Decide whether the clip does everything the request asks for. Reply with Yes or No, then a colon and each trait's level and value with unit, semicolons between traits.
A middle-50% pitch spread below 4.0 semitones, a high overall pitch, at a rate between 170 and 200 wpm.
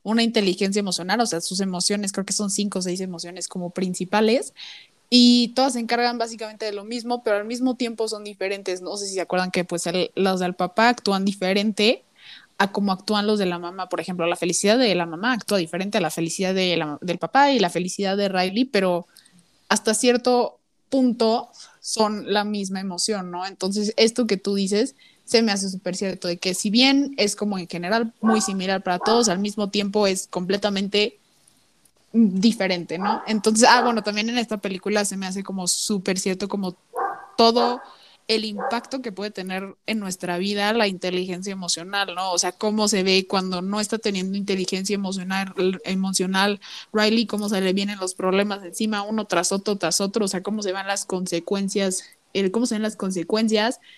Yes: average, 2.8 semitones; high, 200 Hz; fast, 190 wpm